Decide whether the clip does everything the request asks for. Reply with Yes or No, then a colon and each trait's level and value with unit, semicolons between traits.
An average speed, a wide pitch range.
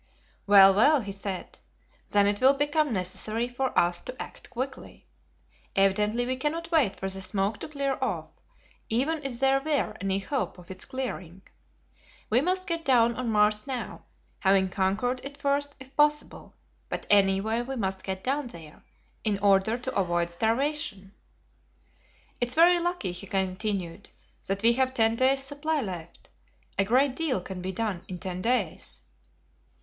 Yes: average, 160 wpm; wide, 5.8 semitones